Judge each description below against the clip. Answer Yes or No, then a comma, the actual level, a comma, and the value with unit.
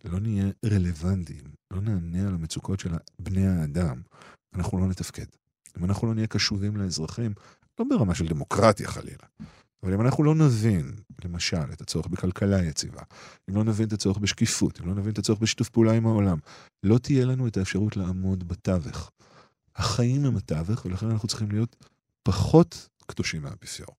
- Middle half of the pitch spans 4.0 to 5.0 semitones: No, average, 3.5 semitones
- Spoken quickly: Yes, fast, 165 wpm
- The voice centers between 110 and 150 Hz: No, low, 100 Hz